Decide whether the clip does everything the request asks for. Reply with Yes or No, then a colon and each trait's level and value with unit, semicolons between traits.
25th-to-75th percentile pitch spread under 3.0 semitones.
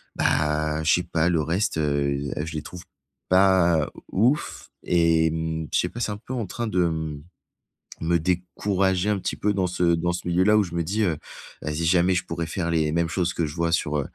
Yes: narrow, 2.6 semitones